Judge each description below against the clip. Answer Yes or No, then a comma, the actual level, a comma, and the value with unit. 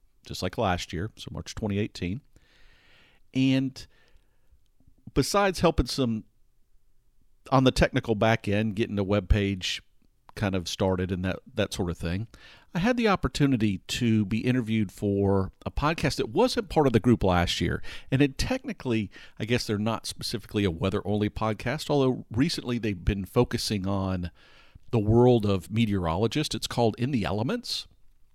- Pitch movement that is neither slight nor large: Yes, average, 4.6 semitones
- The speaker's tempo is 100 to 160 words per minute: Yes, average, 155 wpm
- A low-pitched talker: Yes, low, 110 Hz